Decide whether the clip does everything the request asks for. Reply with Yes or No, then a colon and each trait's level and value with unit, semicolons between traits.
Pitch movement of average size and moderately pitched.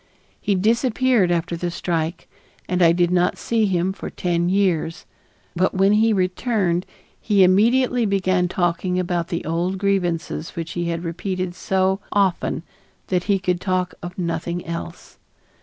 No: narrow, 2.2 semitones; medium, 180 Hz